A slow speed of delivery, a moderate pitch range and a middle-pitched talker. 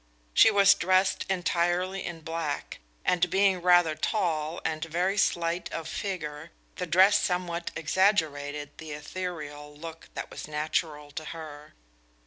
Yes: slow, 130 wpm; average, 3.1 semitones; medium, 165 Hz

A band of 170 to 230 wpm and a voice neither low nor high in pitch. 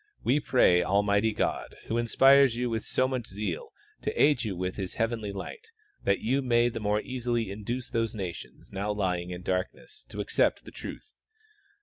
No: average, 185 wpm; low, 110 Hz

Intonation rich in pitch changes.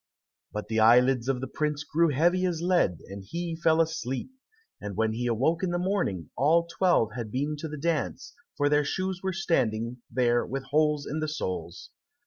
Yes: wide, 6.0 semitones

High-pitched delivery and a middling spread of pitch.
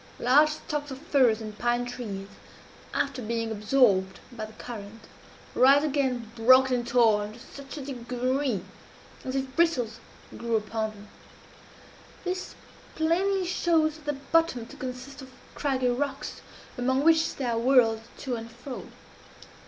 Yes: very high, 255 Hz; average, 3.7 semitones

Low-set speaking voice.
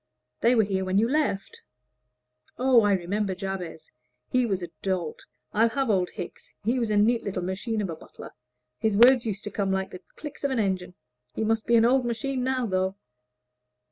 No: high, 210 Hz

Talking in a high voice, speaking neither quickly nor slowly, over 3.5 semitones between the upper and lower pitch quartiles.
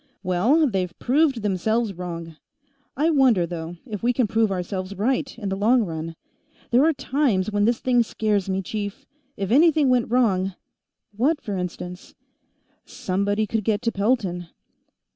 Yes: high, 210 Hz; average, 160 wpm; average, 4.8 semitones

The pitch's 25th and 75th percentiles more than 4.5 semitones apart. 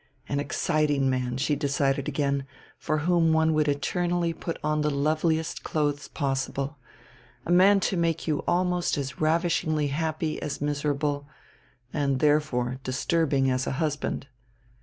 No: narrow, 2.5 semitones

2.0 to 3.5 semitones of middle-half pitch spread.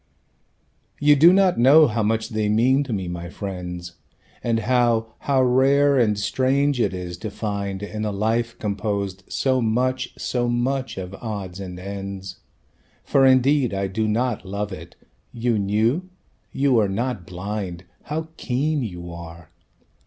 No: average, 4.9 semitones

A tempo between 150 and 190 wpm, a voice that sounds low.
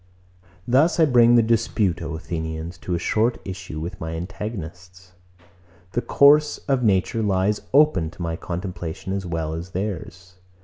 Yes: average, 165 wpm; very low, 95 Hz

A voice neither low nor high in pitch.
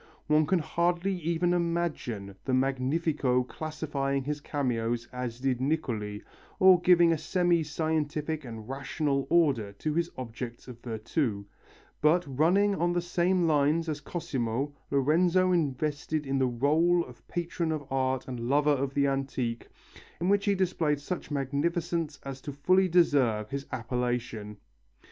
Yes: medium, 145 Hz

